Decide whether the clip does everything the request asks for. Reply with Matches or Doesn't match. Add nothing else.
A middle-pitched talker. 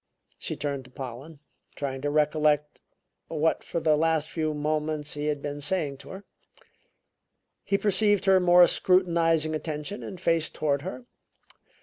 Matches